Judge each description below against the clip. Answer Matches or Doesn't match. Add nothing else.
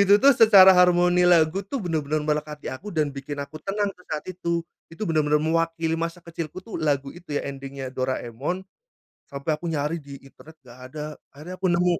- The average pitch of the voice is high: Doesn't match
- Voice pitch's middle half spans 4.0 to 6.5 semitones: Doesn't match